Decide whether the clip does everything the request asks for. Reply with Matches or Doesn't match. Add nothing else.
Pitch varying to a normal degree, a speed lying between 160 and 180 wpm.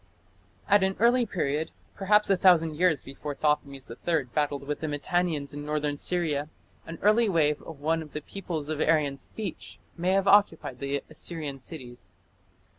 Matches